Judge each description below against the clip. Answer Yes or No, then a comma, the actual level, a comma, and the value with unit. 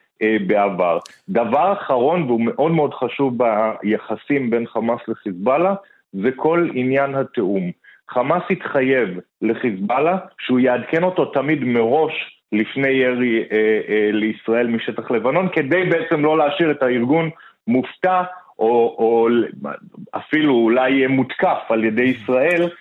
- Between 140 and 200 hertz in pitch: No, low, 125 Hz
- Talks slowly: No, average, 115 wpm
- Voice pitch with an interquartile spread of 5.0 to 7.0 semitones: Yes, wide, 5.5 semitones